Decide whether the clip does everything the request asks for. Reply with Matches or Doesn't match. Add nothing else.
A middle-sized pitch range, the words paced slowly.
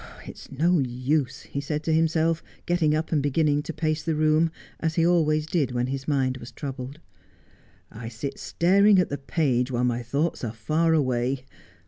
Doesn't match